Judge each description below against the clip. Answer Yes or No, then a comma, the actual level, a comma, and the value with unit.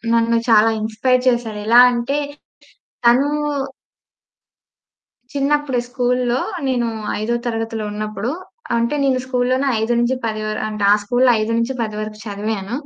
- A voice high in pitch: Yes, high, 235 Hz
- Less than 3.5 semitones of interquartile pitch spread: Yes, narrow, 2.6 semitones